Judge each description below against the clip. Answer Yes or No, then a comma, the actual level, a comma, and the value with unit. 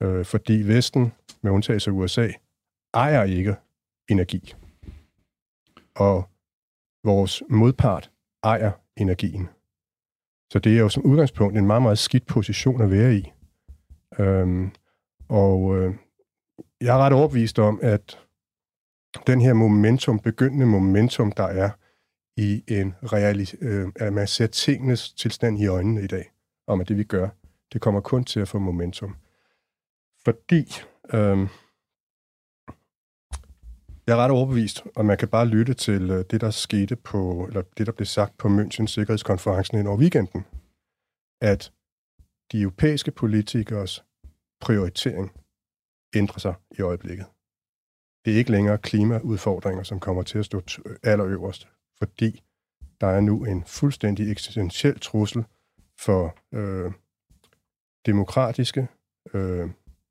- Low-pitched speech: Yes, low, 105 Hz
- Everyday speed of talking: No, slow, 125 wpm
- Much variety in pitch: No, average, 3.2 semitones